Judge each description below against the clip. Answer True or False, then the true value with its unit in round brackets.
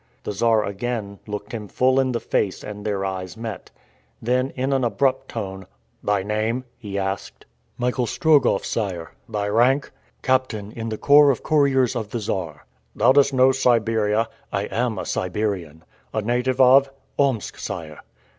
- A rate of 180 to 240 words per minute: False (160 wpm)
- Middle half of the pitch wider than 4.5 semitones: False (4.2 semitones)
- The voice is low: True (115 Hz)